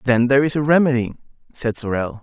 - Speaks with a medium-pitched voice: No, low, 130 Hz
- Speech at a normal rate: Yes, average, 190 wpm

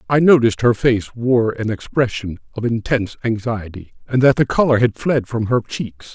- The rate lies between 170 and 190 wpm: Yes, average, 185 wpm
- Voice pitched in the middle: No, low, 115 Hz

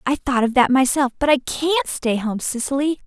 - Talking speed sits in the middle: Yes, average, 195 wpm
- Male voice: No, female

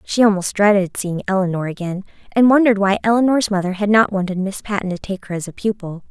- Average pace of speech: No, fast, 215 wpm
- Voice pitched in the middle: No, high, 200 Hz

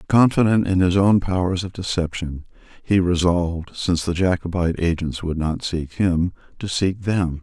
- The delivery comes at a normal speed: Yes, average, 160 wpm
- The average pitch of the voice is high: No, very low, 90 Hz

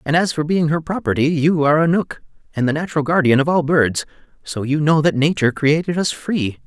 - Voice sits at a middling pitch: Yes, medium, 155 Hz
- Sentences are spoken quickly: Yes, fast, 225 wpm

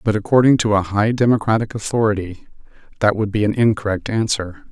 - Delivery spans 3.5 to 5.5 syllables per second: No, 5.9 syllables/s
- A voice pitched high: No, low, 110 Hz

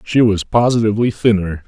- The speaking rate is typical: Yes, average, 145 wpm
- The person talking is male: Yes, male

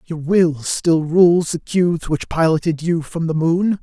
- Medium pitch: Yes, medium, 165 Hz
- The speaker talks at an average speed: Yes, average, 190 wpm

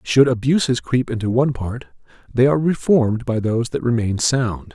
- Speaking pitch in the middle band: No, low, 125 Hz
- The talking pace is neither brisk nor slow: Yes, average, 175 wpm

